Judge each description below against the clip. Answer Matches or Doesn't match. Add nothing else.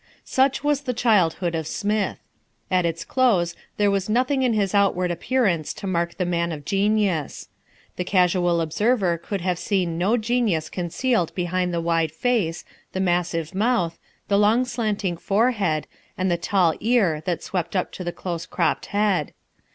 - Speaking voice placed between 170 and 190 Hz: Matches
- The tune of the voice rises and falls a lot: Doesn't match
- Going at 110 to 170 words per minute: Matches